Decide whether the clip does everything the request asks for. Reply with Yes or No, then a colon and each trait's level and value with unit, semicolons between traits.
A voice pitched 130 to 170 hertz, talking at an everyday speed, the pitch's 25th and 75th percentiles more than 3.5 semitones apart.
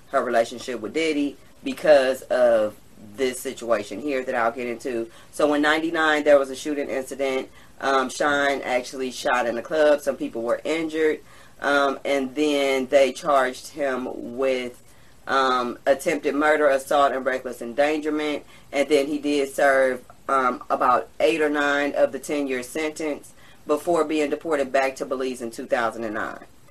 No: medium, 140 Hz; average, 155 wpm; narrow, 2.5 semitones